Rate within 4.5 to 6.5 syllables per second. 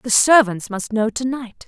No: 4.3 syllables/s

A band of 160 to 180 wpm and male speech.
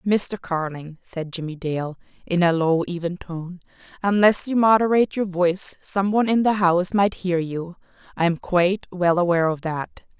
No: average, 170 wpm; female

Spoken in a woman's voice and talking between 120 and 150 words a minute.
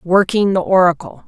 Yes: female; average, 140 wpm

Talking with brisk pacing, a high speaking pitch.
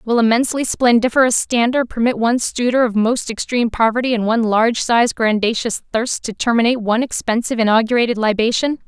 No: average, 150 wpm; high, 235 Hz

